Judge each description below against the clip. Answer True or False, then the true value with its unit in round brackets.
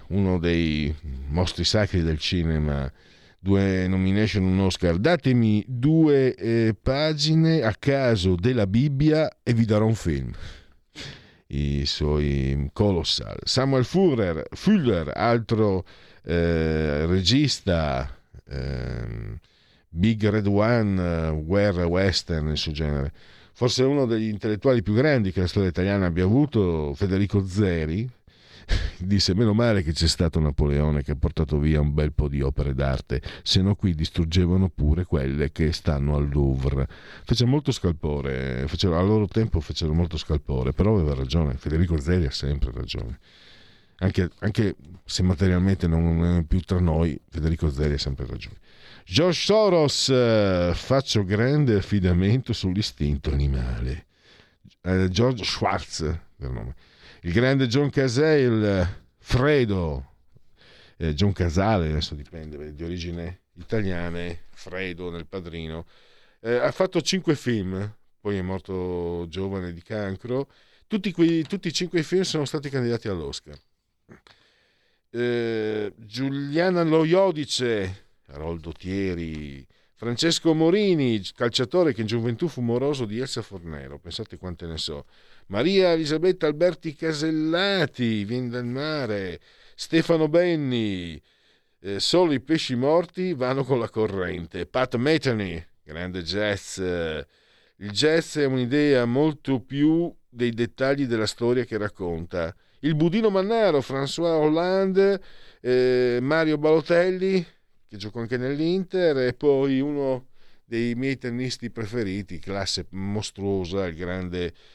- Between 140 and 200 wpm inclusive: False (125 wpm)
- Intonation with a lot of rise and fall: True (7.5 semitones)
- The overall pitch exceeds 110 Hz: False (100 Hz)